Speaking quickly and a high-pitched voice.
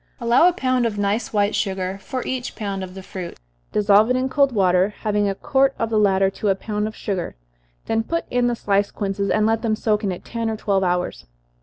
Yes: fast, 230 wpm; high, 210 Hz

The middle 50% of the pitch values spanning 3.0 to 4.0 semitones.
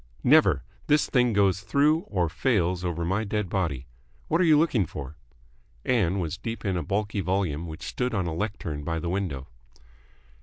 No: average, 4.6 semitones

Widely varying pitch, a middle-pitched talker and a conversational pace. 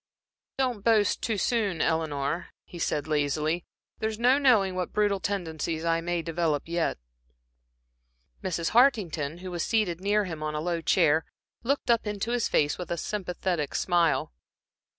No: average, 4.6 semitones; medium, 175 Hz; average, 150 wpm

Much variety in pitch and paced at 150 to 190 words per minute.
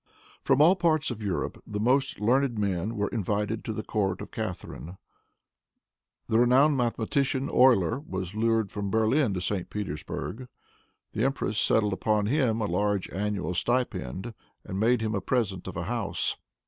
No: average, 3.9 semitones; average, 160 wpm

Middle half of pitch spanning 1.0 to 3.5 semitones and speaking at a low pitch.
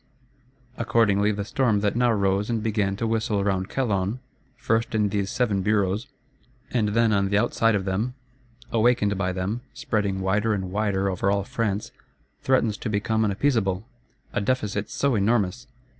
Yes: narrow, 2.5 semitones; low, 105 Hz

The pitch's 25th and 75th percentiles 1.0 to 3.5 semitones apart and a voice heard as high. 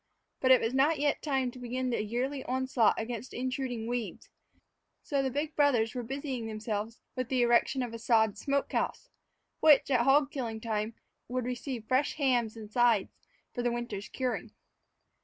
Yes: average, 2.8 semitones; high, 245 Hz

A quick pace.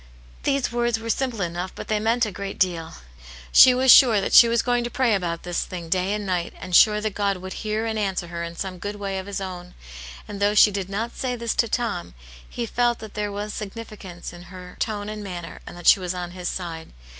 Yes: fast, 240 wpm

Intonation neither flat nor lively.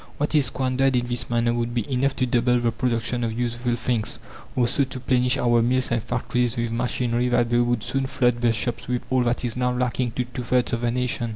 No: narrow, 1.1 semitones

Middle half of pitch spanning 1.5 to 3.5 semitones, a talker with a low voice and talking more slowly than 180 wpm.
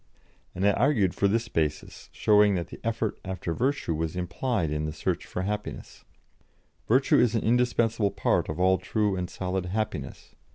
No: average, 4.2 semitones; low, 100 Hz; average, 170 wpm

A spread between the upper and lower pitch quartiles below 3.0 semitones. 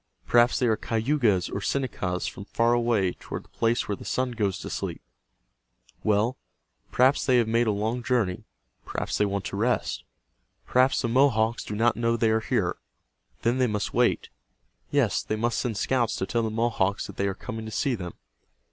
Yes: narrow, 2.6 semitones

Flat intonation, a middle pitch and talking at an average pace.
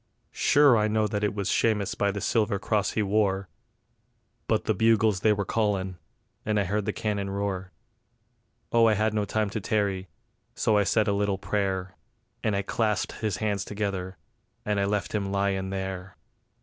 No: narrow, 1.7 semitones; low, 100 Hz; average, 180 wpm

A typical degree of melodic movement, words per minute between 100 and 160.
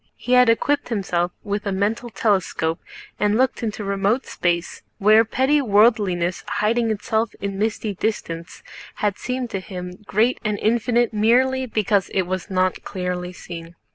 Yes: average, 3.7 semitones; average, 150 wpm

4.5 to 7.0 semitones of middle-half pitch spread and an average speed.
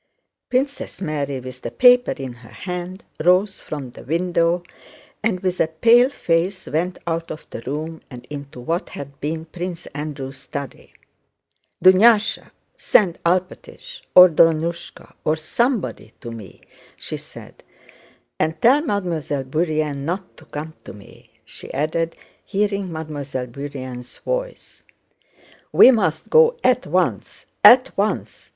No: average, 5.1 semitones; slow, 130 wpm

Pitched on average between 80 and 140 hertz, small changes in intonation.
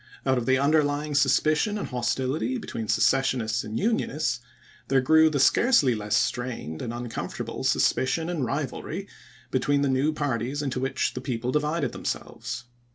No: low, 135 Hz; average, 3.7 semitones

